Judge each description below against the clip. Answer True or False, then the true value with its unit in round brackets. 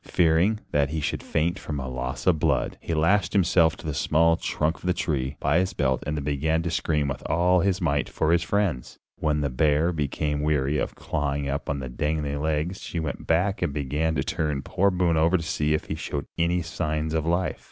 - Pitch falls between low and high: False (80 Hz)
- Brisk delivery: True (220 wpm)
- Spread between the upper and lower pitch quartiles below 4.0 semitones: True (2.7 semitones)